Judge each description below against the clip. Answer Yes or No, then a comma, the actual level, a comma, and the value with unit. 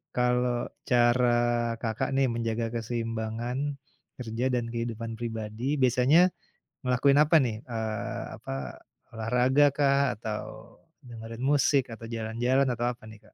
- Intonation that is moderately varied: No, narrow, 2.0 semitones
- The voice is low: Yes, low, 120 Hz